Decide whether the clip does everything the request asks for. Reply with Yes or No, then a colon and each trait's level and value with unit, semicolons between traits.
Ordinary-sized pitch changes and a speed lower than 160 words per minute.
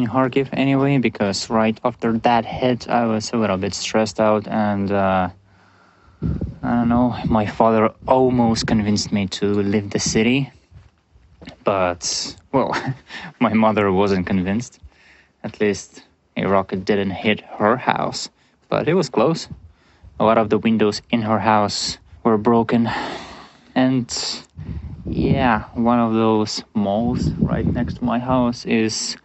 Yes: average, 3.2 semitones; average, 140 wpm